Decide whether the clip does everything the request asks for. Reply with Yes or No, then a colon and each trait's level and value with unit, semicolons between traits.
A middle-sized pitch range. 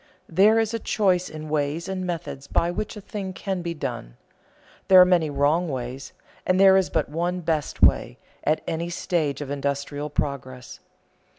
Yes: average, 4.4 semitones